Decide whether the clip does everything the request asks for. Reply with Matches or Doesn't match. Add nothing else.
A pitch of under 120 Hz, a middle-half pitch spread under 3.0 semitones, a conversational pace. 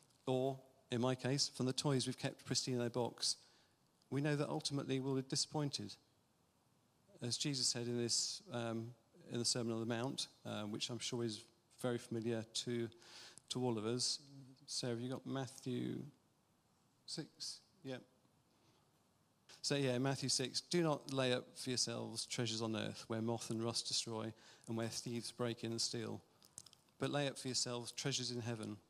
Doesn't match